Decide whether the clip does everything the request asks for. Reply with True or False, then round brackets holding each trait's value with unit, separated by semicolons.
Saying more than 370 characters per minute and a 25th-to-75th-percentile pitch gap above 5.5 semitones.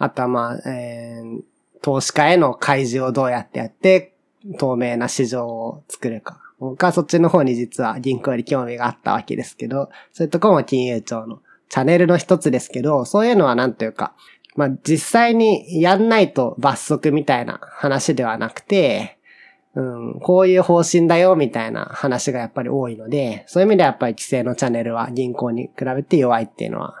True (385 characters per minute; 6.0 semitones)